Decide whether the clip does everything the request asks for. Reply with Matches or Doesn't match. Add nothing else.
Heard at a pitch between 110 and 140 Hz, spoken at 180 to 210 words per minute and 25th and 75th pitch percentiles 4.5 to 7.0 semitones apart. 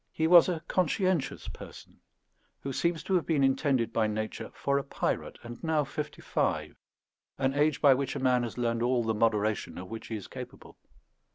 Matches